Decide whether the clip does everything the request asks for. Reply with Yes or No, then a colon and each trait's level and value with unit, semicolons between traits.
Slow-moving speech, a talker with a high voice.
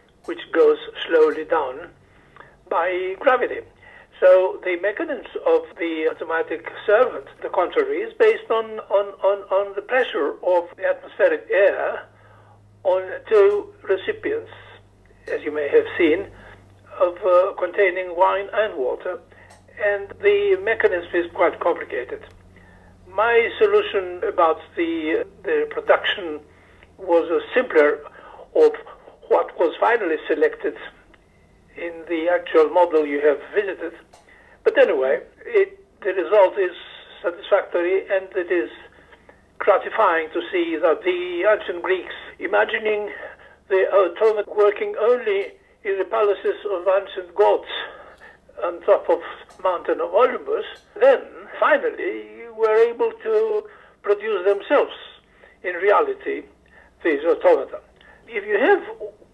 Yes: slow, 120 wpm; very high, 395 Hz